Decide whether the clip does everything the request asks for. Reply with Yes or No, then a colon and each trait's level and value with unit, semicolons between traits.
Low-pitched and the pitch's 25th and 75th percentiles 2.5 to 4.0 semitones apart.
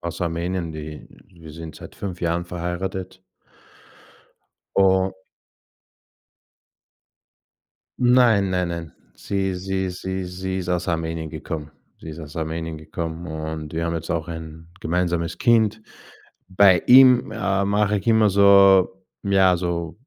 Yes: very low, 90 Hz; average, 2.8 semitones